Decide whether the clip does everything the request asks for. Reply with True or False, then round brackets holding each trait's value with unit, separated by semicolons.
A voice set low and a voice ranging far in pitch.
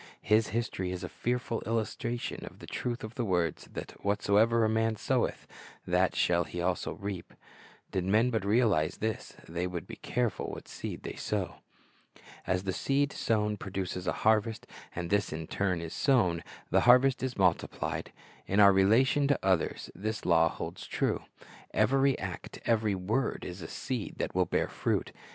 False (105 Hz; 4.1 semitones)